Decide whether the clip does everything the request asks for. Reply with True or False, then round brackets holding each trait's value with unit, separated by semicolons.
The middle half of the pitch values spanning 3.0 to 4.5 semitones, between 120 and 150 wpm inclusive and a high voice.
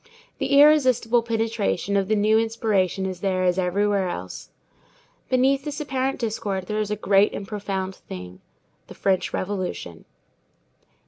True (3.4 semitones; 140 wpm; 205 Hz)